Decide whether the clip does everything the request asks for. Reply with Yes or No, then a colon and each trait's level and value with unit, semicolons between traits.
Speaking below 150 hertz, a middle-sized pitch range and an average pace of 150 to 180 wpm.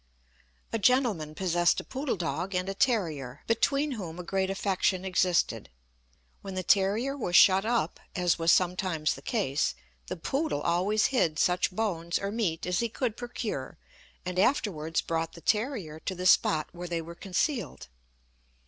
No: medium, 185 Hz; average, 4.5 semitones; average, 160 wpm